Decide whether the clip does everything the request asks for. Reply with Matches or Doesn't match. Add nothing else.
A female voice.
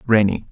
Doesn't match